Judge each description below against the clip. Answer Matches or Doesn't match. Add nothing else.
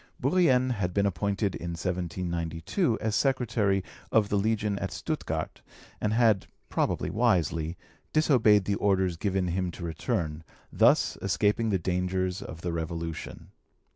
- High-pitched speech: Doesn't match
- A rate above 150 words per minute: Doesn't match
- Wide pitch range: Doesn't match